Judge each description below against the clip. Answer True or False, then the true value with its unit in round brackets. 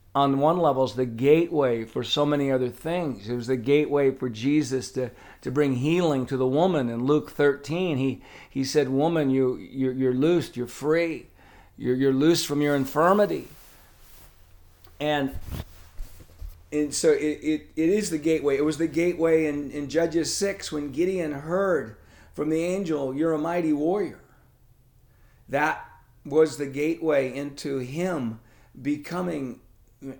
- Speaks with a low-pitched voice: False (145 Hz)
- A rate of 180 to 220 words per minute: False (155 wpm)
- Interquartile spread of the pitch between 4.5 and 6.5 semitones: False (3.8 semitones)